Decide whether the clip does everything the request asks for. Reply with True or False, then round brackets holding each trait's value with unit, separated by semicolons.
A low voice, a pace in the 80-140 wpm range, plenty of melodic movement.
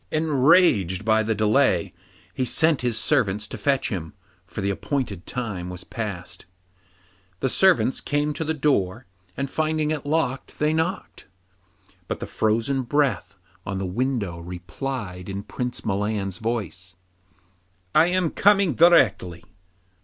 True (120 Hz; 135 wpm; 7.3 semitones)